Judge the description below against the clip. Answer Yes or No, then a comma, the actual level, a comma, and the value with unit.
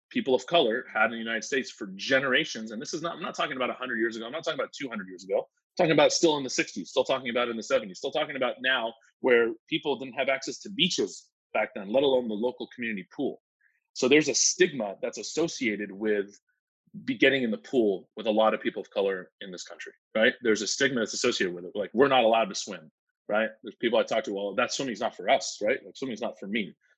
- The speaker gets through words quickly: Yes, fast, 255 wpm